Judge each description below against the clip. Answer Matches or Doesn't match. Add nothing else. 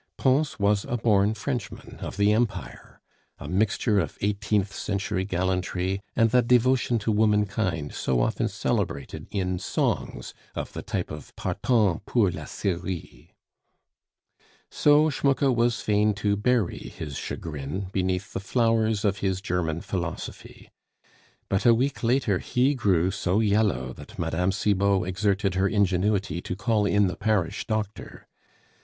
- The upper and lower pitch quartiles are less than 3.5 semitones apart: Matches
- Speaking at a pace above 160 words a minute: Doesn't match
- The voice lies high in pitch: Doesn't match